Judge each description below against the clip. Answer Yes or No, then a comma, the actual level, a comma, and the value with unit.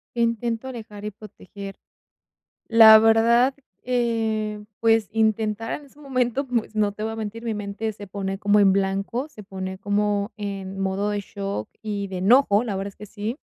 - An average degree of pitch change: No, narrow, 2.2 semitones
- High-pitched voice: Yes, high, 215 Hz